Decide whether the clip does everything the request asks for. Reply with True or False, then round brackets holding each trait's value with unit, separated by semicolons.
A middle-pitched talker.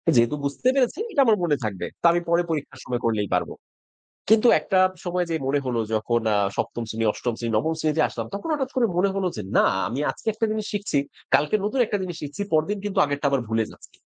True (160 Hz)